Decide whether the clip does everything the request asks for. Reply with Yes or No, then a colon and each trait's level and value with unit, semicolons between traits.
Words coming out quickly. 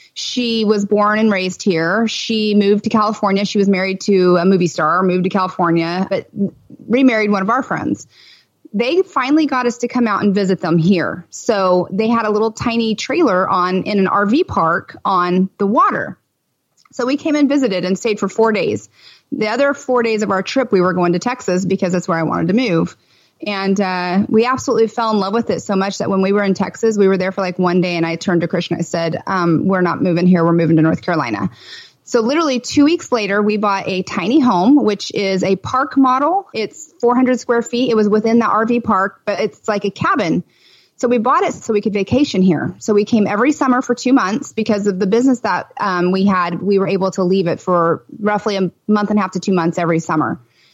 Yes: fast, 230 wpm